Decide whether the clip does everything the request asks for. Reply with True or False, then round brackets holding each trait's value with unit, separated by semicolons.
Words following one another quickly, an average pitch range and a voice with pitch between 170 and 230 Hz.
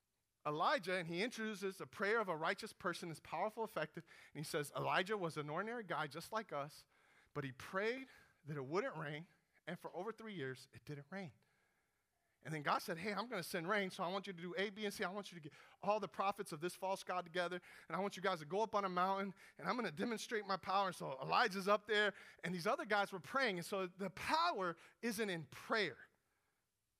True (240 wpm; 3.7 semitones; 190 Hz)